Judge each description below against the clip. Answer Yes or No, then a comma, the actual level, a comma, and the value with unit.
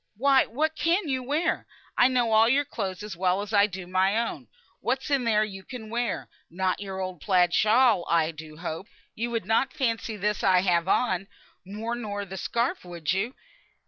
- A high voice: Yes, high, 210 Hz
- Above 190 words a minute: Yes, average, 200 wpm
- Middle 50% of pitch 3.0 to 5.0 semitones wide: Yes, average, 4.6 semitones